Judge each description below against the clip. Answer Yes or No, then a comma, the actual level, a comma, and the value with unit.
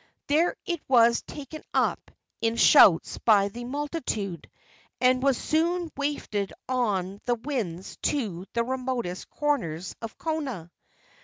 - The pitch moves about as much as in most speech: No, wide, 6.4 semitones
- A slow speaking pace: Yes, slow, 125 wpm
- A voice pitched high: Yes, high, 245 Hz